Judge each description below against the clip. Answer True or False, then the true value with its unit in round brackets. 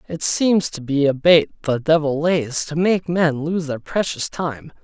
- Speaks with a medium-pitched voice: True (155 Hz)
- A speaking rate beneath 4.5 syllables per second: True (4.1 syllables/s)